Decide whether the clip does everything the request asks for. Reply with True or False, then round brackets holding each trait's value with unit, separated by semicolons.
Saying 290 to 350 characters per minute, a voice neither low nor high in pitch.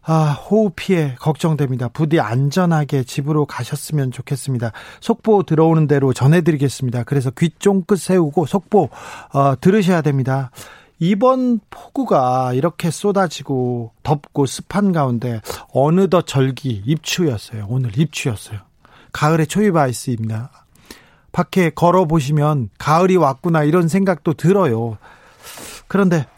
True (305 characters per minute; 155 Hz)